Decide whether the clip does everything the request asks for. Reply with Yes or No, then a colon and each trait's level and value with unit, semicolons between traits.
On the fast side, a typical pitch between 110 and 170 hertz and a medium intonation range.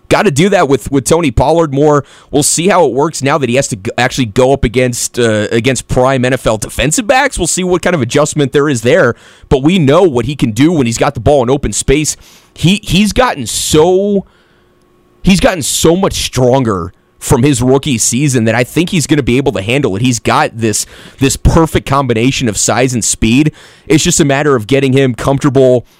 Yes: fast, 220 wpm; low, 135 Hz; average, 3.9 semitones